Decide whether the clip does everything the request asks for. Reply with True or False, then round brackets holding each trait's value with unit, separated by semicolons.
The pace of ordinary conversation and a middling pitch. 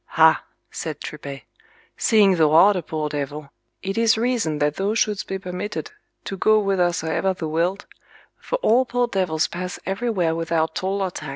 True (170 wpm; 180 Hz)